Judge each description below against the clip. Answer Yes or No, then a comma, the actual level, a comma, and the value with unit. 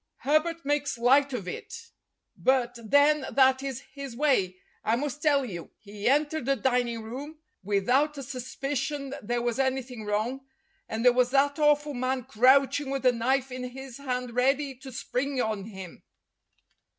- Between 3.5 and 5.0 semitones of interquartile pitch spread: No, average, 2.7 semitones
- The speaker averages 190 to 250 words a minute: No, average, 160 wpm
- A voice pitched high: Yes, very high, 260 Hz